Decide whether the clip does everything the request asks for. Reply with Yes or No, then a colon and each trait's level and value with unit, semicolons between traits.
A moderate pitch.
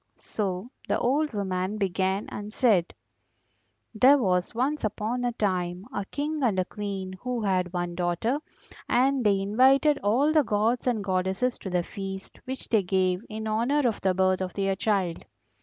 No: high, 205 Hz